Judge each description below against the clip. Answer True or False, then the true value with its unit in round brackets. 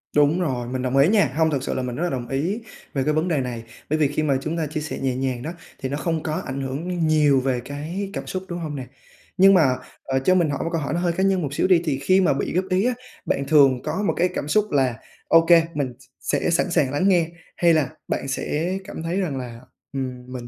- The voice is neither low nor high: True (150 Hz)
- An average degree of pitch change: True (4.4 semitones)